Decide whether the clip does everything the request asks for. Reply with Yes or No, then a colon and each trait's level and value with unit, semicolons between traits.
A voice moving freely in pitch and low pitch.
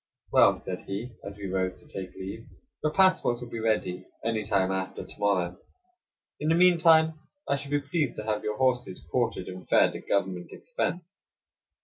Yes: wide, 7.7 semitones; low, 110 Hz